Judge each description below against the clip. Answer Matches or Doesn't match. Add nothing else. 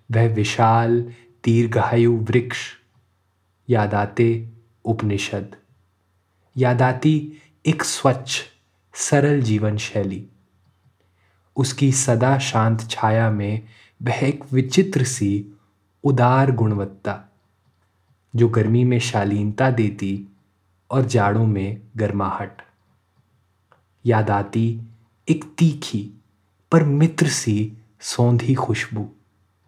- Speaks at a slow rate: Matches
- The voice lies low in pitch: Matches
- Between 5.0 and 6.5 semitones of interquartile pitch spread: Doesn't match